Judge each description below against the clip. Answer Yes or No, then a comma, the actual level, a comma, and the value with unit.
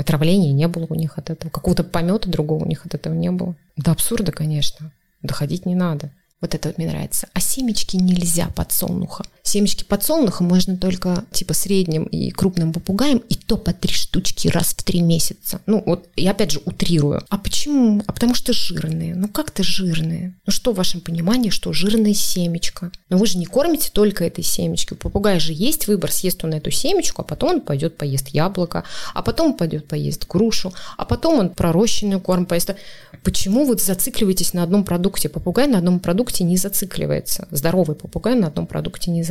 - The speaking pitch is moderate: Yes, medium, 180 Hz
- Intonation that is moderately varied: Yes, average, 3.6 semitones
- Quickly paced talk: Yes, fast, 190 wpm